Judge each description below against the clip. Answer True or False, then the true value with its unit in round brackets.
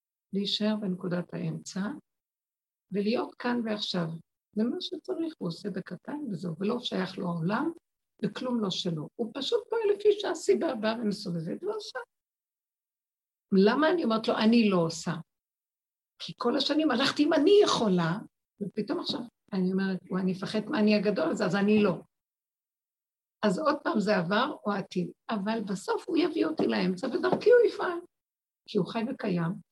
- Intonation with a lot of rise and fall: True (7.5 semitones)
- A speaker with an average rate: False (155 wpm)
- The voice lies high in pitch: True (215 Hz)